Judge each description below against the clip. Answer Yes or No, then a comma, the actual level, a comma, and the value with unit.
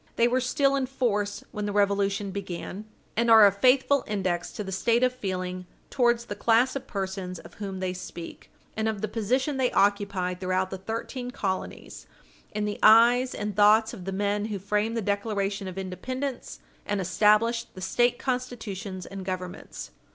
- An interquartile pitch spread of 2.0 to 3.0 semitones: No, average, 3.6 semitones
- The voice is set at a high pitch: Yes, high, 205 Hz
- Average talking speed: Yes, average, 175 wpm